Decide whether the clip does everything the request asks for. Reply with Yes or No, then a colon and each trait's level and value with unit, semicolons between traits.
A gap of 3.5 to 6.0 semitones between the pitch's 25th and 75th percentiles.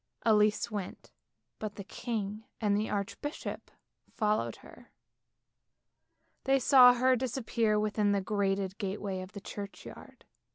No: narrow, 2.4 semitones